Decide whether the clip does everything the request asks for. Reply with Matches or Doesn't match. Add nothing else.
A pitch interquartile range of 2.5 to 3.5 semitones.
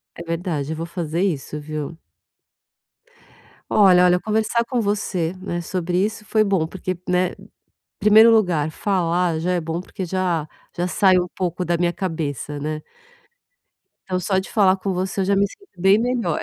Matches